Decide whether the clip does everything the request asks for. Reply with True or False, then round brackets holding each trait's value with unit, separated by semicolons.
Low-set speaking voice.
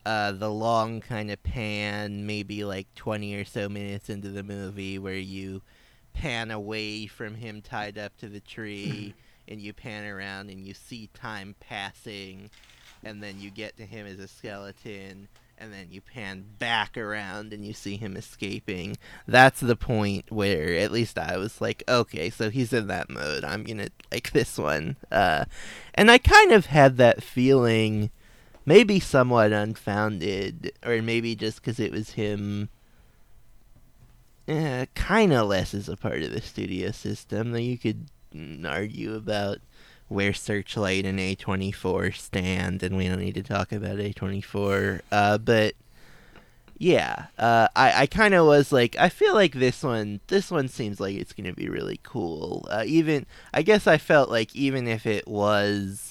True (105 Hz)